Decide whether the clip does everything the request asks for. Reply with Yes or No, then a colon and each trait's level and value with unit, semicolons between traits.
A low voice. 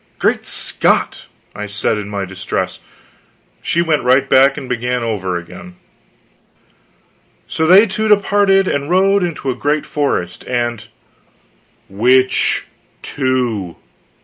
Yes: low, 130 Hz